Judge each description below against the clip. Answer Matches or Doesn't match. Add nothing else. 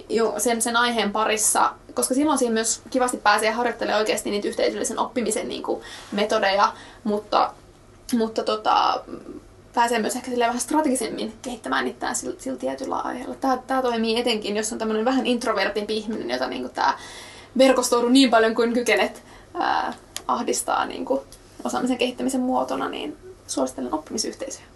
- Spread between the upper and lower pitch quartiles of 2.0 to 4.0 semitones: Matches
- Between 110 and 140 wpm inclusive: Doesn't match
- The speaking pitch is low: Doesn't match